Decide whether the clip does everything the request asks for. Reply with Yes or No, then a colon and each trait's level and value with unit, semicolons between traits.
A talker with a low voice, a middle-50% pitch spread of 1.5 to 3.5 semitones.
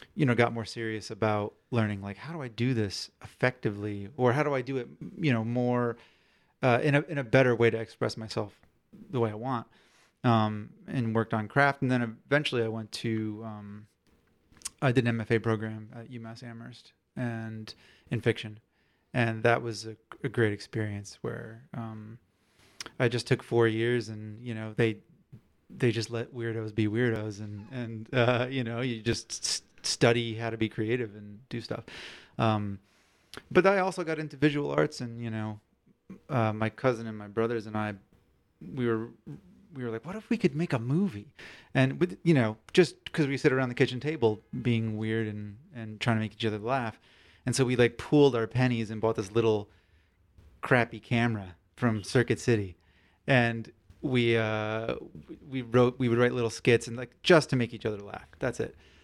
Yes: low, 115 Hz; narrow, 2.6 semitones